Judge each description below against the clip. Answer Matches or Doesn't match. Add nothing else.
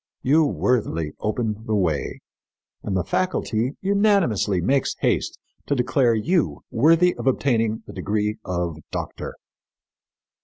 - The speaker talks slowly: Matches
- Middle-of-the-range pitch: Doesn't match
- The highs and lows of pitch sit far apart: Matches